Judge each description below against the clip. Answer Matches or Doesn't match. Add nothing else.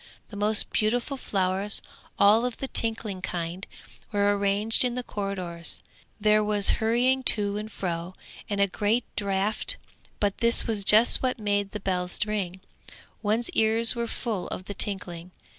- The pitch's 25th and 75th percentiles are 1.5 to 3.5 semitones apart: Matches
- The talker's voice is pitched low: Doesn't match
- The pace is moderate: Matches